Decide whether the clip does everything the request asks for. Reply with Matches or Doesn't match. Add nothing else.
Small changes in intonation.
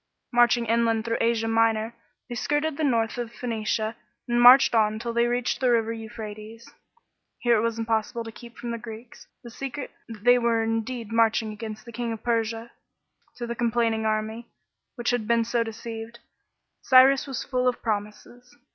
Matches